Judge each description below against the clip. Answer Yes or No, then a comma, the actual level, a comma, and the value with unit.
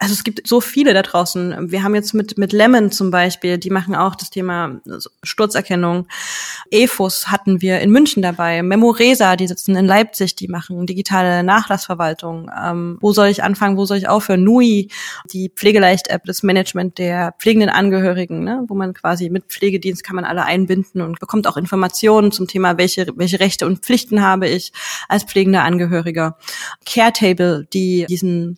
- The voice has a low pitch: No, high, 190 Hz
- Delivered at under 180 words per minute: Yes, average, 170 wpm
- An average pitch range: No, narrow, 2.2 semitones